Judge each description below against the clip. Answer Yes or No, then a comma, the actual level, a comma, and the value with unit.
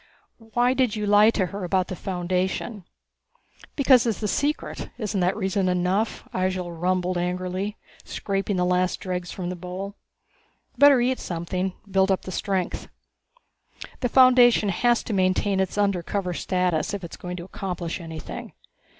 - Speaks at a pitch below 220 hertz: Yes, high, 190 Hz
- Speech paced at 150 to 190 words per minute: Yes, average, 155 wpm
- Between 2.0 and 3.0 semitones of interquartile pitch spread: Yes, narrow, 2.6 semitones